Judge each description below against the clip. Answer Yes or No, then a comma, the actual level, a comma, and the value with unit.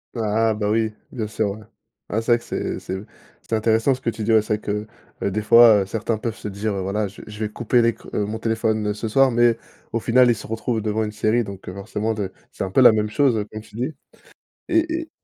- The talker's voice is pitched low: Yes, low, 110 Hz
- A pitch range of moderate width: No, narrow, 1.8 semitones